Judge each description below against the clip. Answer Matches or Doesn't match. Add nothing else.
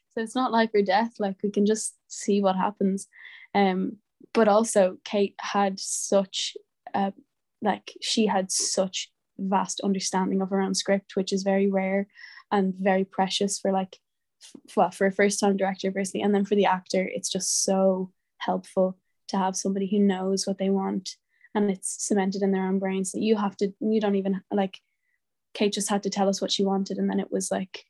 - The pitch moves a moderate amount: Doesn't match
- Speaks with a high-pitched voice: Matches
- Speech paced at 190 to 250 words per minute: Matches